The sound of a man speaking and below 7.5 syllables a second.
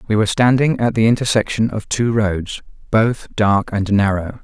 Yes: male; 4.9 syllables/s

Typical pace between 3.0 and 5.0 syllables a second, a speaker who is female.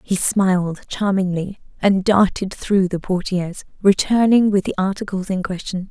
Yes: 4.7 syllables/s; female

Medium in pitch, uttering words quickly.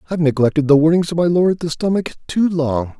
Yes: medium, 160 Hz; fast, 220 wpm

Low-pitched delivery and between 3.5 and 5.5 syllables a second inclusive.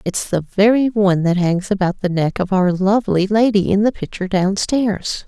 No: high, 200 Hz; 5.0 syllables/s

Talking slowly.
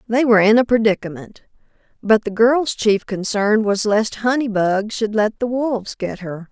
No: average, 185 wpm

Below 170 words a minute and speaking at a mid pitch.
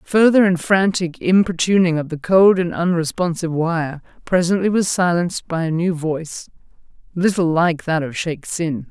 Yes: average, 155 wpm; medium, 170 Hz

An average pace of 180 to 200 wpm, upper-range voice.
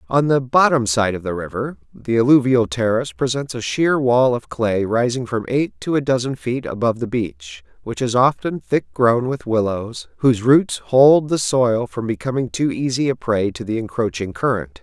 No: average, 195 wpm; low, 120 Hz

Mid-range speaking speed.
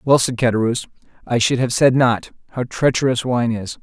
Yes: average, 175 wpm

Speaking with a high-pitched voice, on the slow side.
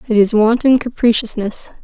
Yes: high, 225 Hz; slow, 130 wpm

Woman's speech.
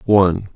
No: male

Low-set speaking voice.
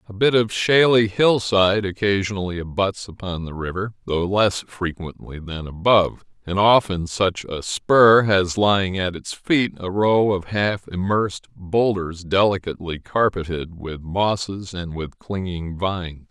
Yes: very low, 95 Hz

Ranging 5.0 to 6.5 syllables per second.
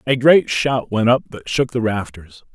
No: 4.5 syllables/s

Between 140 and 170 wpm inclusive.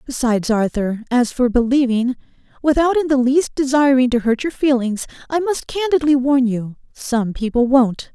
Yes: average, 145 wpm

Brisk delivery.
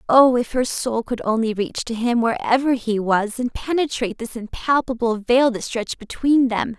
No: average, 185 wpm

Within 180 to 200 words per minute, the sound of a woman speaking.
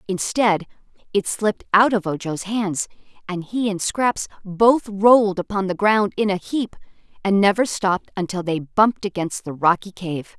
No: average, 170 wpm; female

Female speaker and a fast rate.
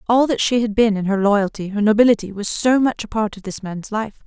Yes: female; fast, 265 wpm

